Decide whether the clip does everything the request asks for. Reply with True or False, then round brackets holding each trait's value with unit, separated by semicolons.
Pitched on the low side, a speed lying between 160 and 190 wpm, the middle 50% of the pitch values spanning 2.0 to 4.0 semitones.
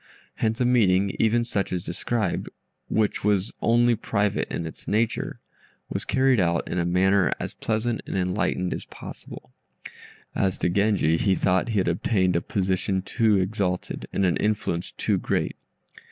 True (100 Hz; 165 wpm; 3.2 semitones)